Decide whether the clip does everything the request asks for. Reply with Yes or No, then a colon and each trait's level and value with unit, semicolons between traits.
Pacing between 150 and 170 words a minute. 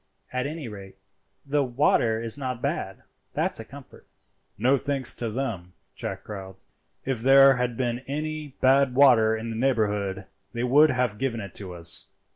Yes: average, 165 wpm